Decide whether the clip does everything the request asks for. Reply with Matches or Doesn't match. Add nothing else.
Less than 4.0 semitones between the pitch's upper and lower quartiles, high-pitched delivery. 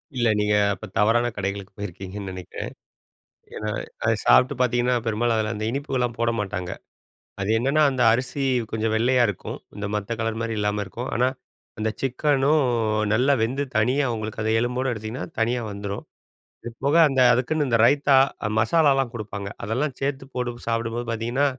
Doesn't match